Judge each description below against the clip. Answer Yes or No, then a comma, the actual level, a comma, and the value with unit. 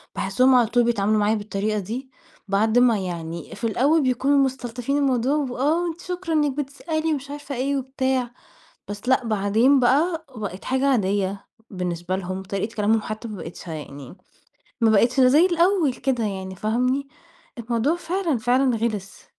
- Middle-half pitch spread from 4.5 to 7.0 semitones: Yes, average, 5.2 semitones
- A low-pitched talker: No, high, 245 Hz